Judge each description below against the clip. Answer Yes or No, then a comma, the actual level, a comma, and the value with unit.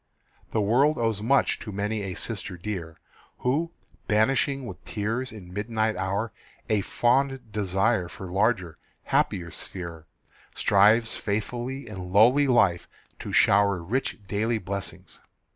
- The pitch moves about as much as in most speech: Yes, average, 3.7 semitones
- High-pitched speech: No, low, 105 Hz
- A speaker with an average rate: No, slow, 125 wpm